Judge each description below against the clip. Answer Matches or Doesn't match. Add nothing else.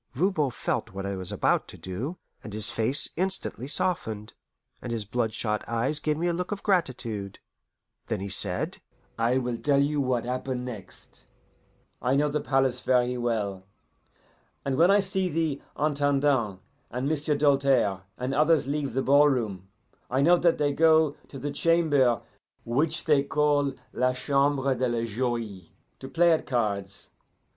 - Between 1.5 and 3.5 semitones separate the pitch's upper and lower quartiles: Doesn't match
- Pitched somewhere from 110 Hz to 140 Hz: Matches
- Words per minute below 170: Matches